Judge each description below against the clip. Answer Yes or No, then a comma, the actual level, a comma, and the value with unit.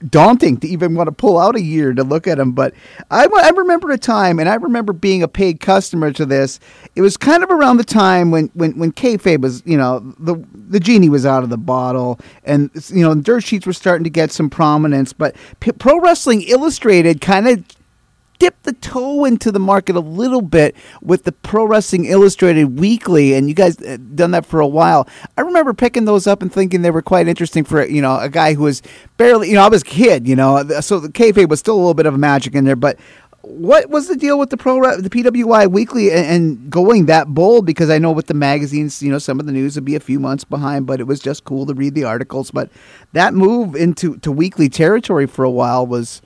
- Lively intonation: Yes, wide, 6.4 semitones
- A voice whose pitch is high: No, medium, 170 Hz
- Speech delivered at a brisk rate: Yes, fast, 240 wpm